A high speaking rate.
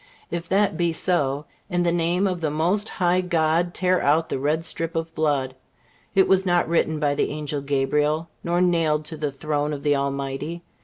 No: average, 195 wpm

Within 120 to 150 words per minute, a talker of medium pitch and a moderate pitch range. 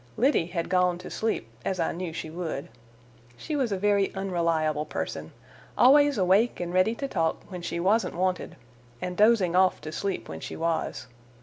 No: average, 180 wpm; medium, 180 Hz; average, 3.5 semitones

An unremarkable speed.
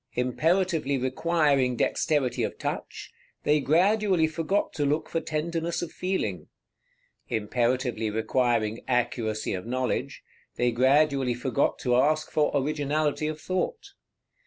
No: slow, 115 wpm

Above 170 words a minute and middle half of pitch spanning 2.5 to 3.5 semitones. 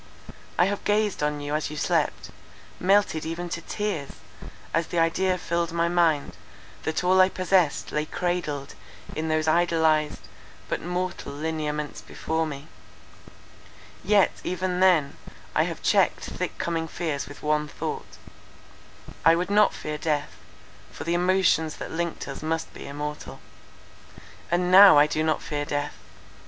No: average, 145 wpm; average, 2.9 semitones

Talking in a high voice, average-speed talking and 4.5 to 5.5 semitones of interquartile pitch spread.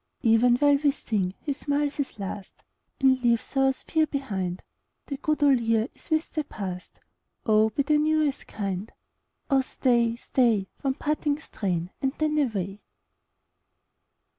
Yes: very high, 260 Hz; average, 160 wpm; average, 5.2 semitones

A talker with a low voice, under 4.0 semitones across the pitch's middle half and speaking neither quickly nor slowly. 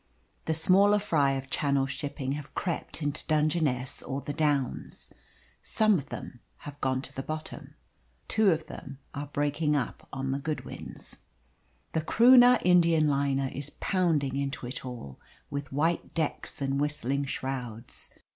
No: medium, 145 Hz; average, 2.8 semitones; average, 145 wpm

